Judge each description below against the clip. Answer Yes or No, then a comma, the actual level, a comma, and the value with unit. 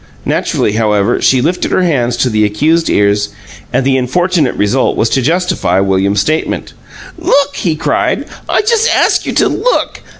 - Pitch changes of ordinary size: No, wide, 8.3 semitones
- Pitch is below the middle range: Yes, low, 130 Hz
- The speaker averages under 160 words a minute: No, average, 165 wpm